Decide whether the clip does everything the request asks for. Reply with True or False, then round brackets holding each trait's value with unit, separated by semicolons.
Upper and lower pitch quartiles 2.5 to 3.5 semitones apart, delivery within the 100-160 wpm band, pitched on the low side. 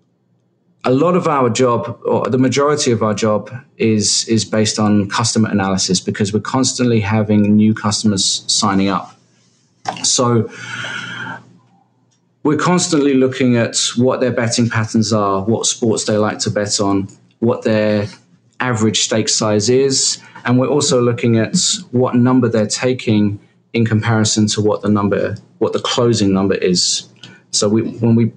True (3.0 semitones; 150 wpm; 110 Hz)